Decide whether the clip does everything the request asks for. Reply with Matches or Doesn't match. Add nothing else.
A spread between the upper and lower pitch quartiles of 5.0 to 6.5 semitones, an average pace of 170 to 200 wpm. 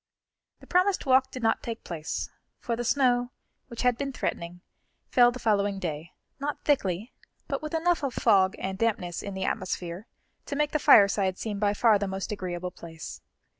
Matches